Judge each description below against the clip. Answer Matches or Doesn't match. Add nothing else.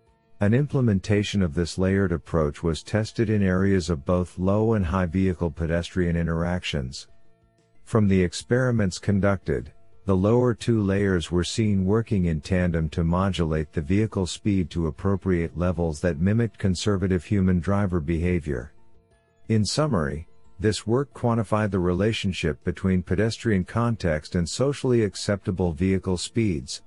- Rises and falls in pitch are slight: Doesn't match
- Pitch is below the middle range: Matches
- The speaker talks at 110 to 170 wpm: Matches